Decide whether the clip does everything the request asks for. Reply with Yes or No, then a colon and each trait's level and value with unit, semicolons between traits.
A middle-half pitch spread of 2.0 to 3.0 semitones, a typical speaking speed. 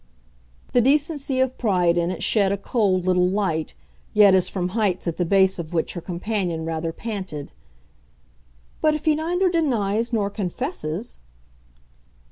No: wide, 5.6 semitones; average, 150 wpm